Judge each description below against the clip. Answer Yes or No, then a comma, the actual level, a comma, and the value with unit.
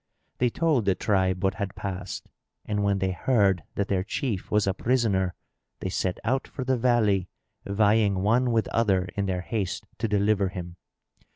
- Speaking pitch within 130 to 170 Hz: No, low, 100 Hz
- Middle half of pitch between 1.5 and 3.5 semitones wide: Yes, average, 3.1 semitones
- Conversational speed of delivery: Yes, average, 175 wpm